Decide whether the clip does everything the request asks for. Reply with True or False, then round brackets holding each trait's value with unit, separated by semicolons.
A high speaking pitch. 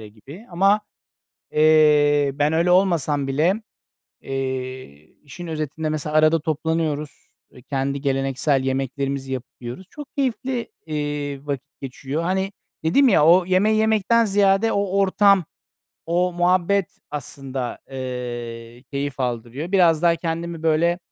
False (155 Hz)